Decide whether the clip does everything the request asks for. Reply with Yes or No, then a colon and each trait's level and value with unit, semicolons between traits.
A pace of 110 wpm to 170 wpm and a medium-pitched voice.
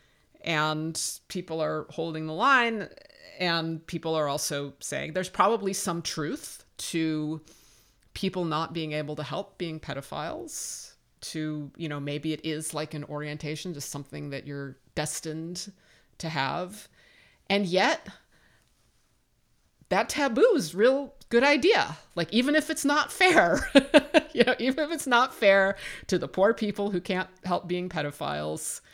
Yes: average, 145 wpm; medium, 170 Hz